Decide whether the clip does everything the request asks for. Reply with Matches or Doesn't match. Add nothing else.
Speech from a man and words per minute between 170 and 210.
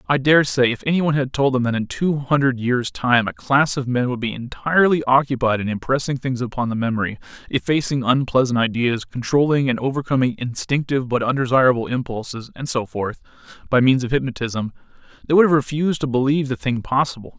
Matches